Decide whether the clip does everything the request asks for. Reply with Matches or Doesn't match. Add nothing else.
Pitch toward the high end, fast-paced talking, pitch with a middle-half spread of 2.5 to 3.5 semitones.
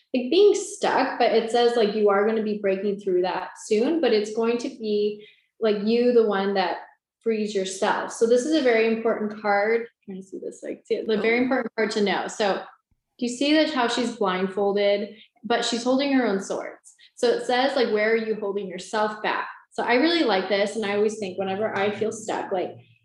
Matches